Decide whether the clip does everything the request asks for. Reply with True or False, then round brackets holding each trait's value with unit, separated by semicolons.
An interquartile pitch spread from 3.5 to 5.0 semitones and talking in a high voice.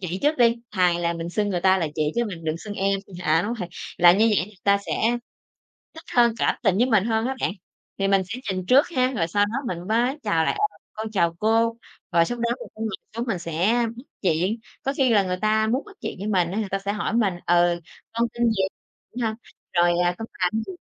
True (4.6 semitones; 205 Hz)